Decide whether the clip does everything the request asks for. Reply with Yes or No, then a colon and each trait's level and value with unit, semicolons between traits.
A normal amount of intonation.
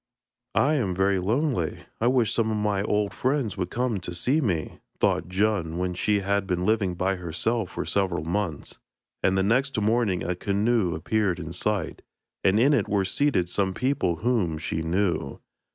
Yes: average, 3.9 semitones